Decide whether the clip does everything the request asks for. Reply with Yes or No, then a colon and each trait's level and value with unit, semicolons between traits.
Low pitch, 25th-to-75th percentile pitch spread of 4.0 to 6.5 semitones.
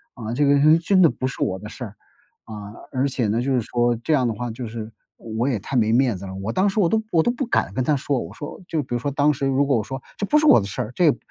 Yes: low, 130 Hz; average, 4.6 semitones